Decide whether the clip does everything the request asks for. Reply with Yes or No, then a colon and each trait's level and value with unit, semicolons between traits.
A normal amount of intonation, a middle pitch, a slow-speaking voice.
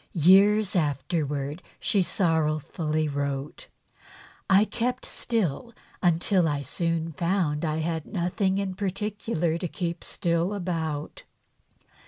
Yes: average, 4.0 semitones; medium, 170 Hz; slow, 110 wpm